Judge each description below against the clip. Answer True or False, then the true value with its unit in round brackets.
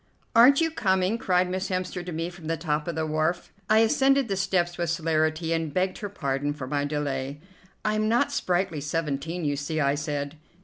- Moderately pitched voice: True (165 Hz)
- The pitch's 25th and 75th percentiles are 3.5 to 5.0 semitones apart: True (4.0 semitones)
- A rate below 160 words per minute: False (205 wpm)